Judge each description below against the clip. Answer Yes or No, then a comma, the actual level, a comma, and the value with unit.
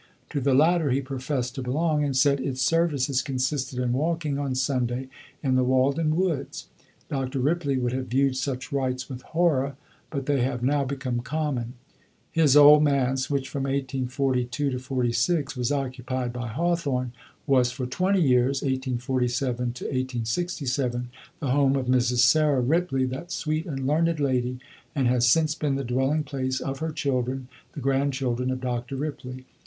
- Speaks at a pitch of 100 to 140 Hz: Yes, low, 135 Hz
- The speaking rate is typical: Yes, average, 160 wpm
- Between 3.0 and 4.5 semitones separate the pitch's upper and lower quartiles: No, narrow, 2.4 semitones